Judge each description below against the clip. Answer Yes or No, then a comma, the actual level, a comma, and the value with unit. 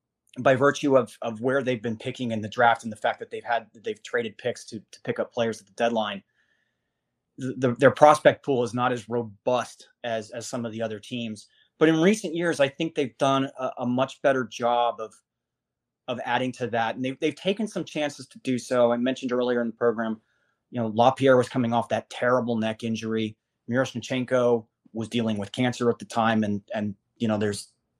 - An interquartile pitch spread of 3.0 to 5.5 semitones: No, narrow, 2.5 semitones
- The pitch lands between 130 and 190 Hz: No, low, 120 Hz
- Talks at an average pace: No, fast, 215 wpm